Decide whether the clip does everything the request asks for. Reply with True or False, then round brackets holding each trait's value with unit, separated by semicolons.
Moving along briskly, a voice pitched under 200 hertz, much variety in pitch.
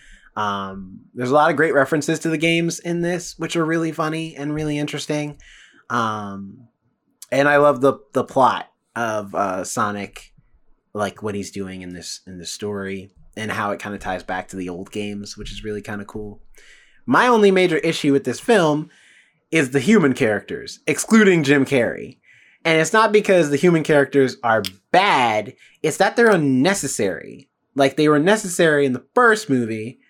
False (180 wpm; 140 Hz; 7.8 semitones)